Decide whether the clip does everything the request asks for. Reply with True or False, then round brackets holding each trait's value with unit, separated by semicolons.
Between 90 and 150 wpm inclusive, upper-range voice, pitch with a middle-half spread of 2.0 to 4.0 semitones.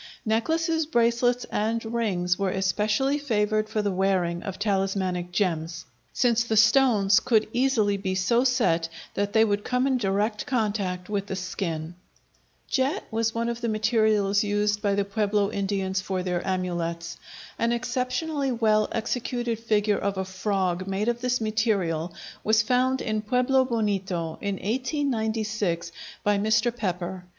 True (145 wpm; 210 Hz; 3.5 semitones)